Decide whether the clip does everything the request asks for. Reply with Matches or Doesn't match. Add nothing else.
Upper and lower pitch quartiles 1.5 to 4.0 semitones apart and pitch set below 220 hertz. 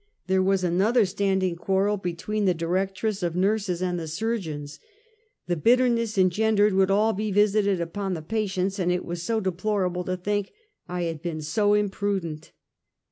Matches